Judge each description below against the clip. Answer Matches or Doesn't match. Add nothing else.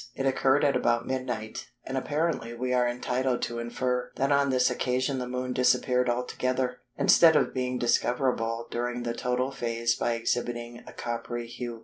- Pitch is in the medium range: Doesn't match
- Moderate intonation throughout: Doesn't match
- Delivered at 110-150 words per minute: Doesn't match